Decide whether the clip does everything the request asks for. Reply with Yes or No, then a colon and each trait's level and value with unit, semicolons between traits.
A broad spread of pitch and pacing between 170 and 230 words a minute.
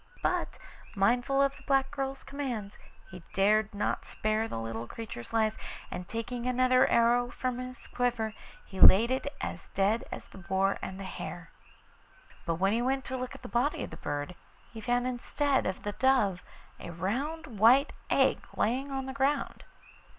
No: average, 4.9 semitones; average, 175 wpm